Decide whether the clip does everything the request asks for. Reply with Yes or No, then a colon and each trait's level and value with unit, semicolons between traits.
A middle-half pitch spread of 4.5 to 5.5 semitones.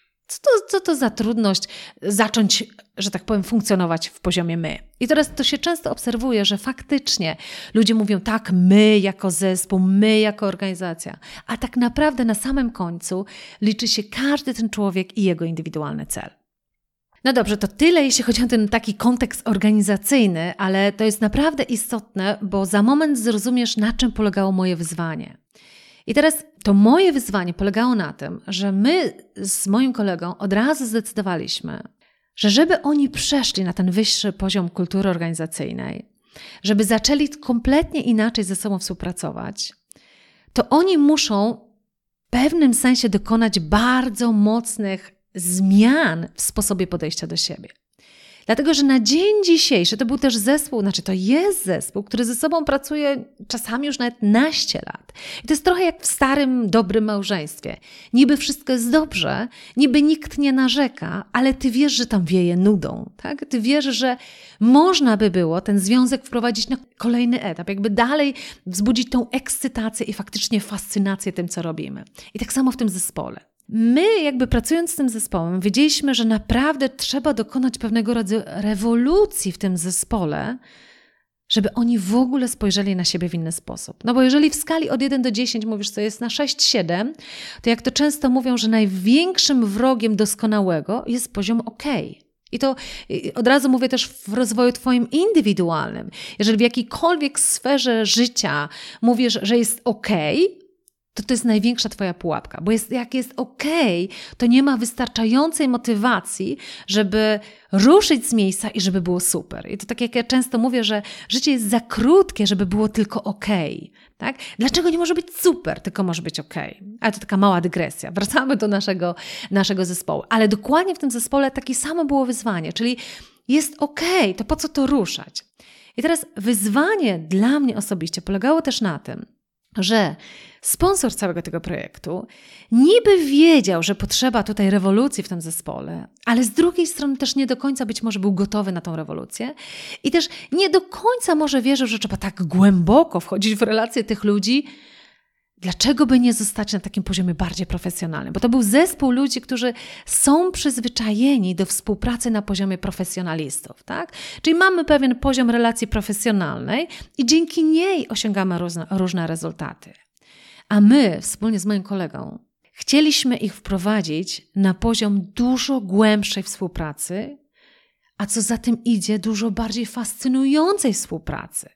Yes: average, 5.1 semitones